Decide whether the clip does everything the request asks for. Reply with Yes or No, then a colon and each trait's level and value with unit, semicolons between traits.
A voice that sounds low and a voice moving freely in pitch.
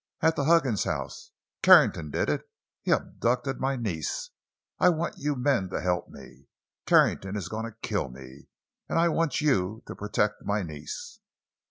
Yes: low, 110 Hz; wide, 7.5 semitones